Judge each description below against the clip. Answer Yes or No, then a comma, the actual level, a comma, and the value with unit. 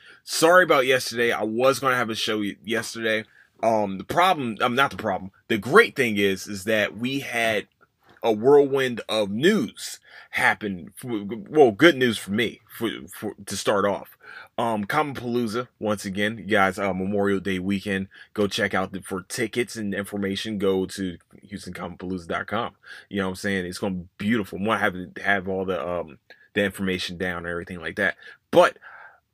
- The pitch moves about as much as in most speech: Yes, average, 3.3 semitones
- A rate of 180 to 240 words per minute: Yes, average, 185 wpm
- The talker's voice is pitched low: Yes, low, 105 Hz